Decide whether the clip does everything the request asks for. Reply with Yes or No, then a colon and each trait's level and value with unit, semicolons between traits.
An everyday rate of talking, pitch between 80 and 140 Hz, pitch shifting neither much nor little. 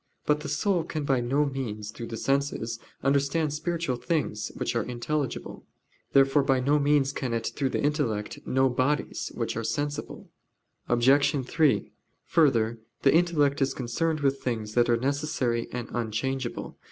Yes: average, 155 wpm; low, 135 Hz; average, 3.6 semitones